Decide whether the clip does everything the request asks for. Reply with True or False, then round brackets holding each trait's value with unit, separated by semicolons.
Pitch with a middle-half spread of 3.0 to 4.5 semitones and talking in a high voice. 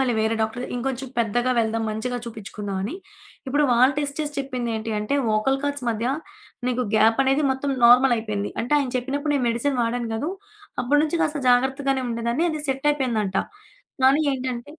True (3.3 semitones; 250 Hz)